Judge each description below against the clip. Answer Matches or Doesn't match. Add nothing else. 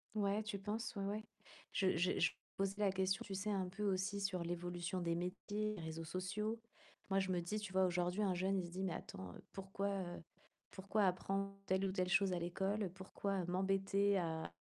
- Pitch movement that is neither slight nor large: Doesn't match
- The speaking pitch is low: Doesn't match